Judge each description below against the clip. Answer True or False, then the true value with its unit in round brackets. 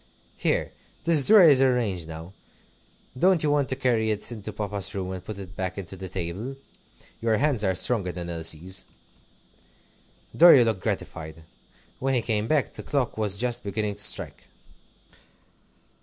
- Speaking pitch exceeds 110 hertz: False (105 Hz)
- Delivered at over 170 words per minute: False (155 wpm)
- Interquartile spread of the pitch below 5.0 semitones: False (5.3 semitones)